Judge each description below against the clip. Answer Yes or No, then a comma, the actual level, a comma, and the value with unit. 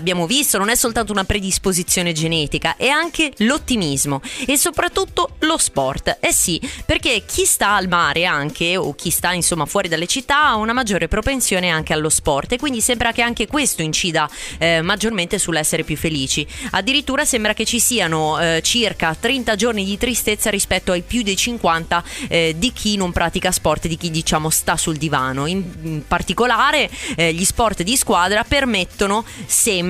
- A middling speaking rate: No, fast, 175 wpm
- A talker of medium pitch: No, high, 195 Hz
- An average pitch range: No, wide, 6.3 semitones